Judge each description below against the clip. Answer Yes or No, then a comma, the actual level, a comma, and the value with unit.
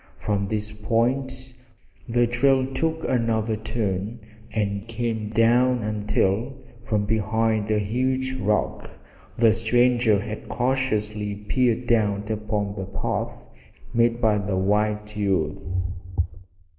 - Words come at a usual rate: No, slow, 110 wpm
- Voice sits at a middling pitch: No, low, 110 Hz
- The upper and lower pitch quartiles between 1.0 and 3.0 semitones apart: Yes, narrow, 2.6 semitones